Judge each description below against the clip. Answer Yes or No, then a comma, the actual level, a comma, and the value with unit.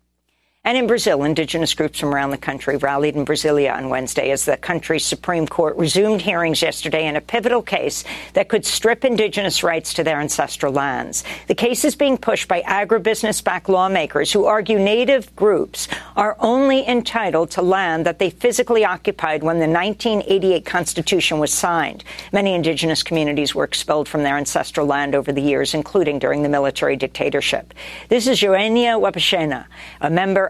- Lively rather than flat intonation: Yes, wide, 6.2 semitones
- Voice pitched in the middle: Yes, medium, 175 Hz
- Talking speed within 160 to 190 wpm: Yes, average, 165 wpm